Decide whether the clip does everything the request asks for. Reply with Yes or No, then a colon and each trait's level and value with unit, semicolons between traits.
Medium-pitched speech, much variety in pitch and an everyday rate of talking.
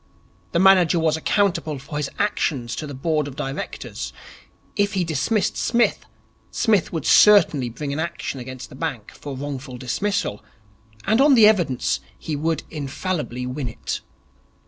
Yes: medium, 155 Hz; wide, 6.0 semitones; average, 150 wpm